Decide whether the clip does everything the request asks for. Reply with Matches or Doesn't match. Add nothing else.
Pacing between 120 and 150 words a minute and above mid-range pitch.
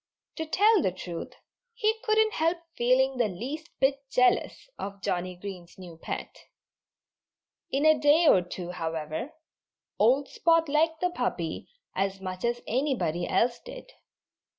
Matches